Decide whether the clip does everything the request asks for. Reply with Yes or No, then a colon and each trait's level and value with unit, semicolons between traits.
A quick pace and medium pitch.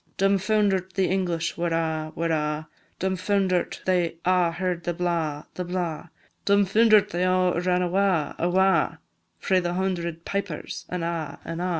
No: average, 145 wpm; medium, 180 Hz